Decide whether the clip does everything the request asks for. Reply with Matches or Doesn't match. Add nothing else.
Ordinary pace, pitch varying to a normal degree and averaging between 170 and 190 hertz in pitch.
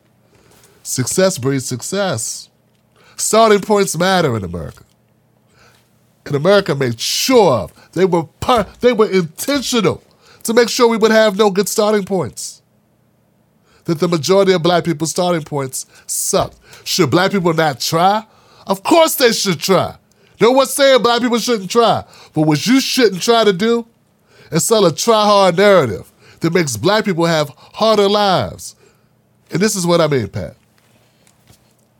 Doesn't match